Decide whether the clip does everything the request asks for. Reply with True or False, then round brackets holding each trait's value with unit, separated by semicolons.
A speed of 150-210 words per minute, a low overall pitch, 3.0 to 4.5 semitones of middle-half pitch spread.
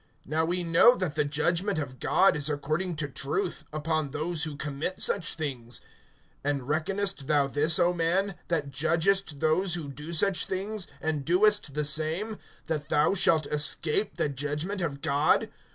False (165 wpm; 155 Hz; 3.4 semitones)